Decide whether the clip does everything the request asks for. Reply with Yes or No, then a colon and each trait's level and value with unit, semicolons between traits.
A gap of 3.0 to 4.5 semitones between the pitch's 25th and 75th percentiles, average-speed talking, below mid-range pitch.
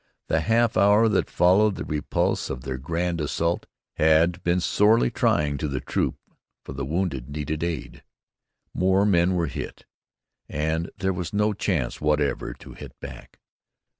Yes: average, 4.1 semitones; average, 155 wpm; very low, 85 Hz